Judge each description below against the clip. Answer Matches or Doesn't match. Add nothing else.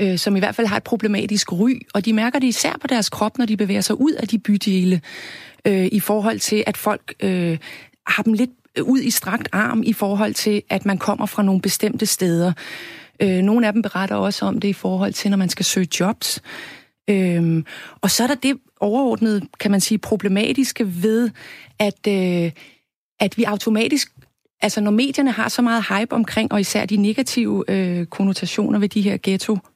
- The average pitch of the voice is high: Matches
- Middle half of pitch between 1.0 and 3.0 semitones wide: Matches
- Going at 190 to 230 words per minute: Matches